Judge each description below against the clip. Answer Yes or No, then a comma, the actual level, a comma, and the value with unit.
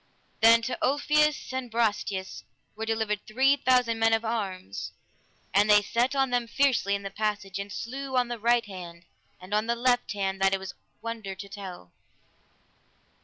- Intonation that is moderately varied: Yes, average, 3.6 semitones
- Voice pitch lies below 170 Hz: No, high, 225 Hz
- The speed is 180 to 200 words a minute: No, average, 170 wpm